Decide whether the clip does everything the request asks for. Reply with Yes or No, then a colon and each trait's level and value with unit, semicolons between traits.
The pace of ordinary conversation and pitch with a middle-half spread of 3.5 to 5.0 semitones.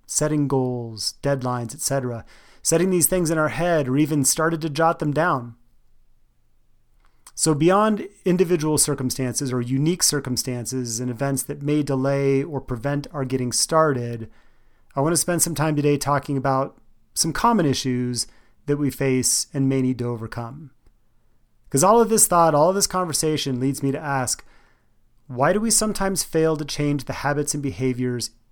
Yes: average, 165 wpm; average, 4.0 semitones